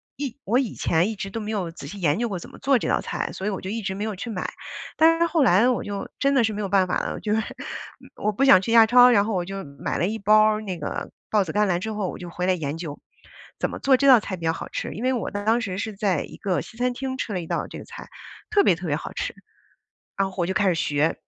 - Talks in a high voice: Yes, high, 205 Hz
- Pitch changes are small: No, average, 4.1 semitones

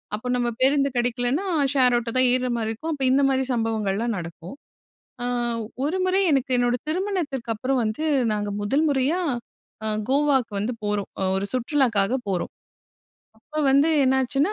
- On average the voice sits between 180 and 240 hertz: No, very high, 255 Hz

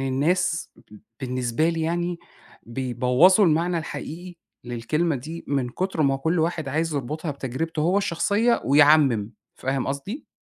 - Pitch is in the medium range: Yes, medium, 155 Hz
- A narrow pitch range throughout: No, average, 4.3 semitones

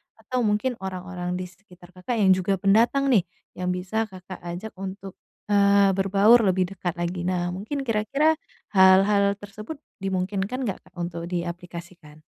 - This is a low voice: No, high, 190 Hz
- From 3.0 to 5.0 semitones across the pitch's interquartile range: No, narrow, 2.6 semitones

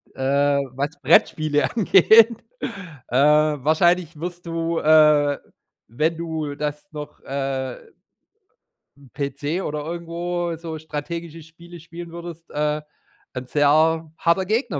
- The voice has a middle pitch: Yes, medium, 155 Hz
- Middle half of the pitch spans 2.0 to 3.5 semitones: Yes, narrow, 2.6 semitones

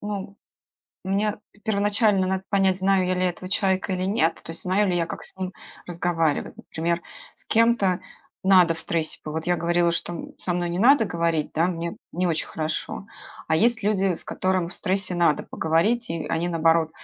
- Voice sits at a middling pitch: Yes, medium, 180 Hz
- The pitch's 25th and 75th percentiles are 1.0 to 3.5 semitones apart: Yes, average, 2.7 semitones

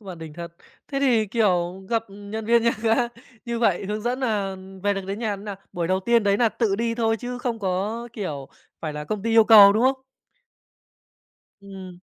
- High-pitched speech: Yes, high, 210 Hz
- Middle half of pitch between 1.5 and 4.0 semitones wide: Yes, average, 3.4 semitones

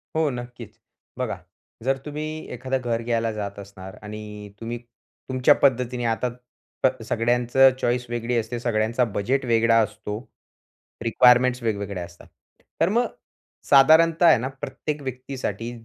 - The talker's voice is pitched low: Yes, low, 120 Hz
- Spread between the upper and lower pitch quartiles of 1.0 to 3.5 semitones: Yes, average, 2.9 semitones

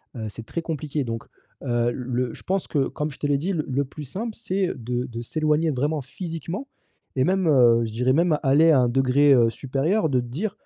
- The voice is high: No, medium, 140 Hz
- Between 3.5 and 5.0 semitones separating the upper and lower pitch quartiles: Yes, average, 4.7 semitones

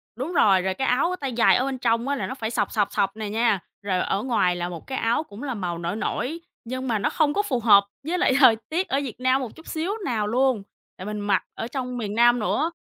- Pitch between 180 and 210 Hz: No, high, 240 Hz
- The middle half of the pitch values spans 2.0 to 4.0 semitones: No, average, 4.5 semitones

